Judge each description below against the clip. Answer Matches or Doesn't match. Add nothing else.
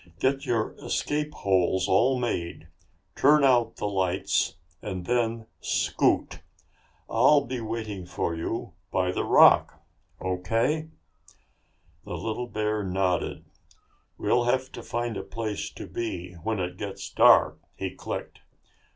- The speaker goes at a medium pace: Doesn't match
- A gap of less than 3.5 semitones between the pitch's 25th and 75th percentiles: Doesn't match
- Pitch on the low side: Matches